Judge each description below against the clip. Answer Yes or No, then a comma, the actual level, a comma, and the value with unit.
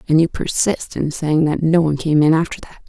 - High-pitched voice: No, medium, 155 Hz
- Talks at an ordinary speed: No, fast, 250 wpm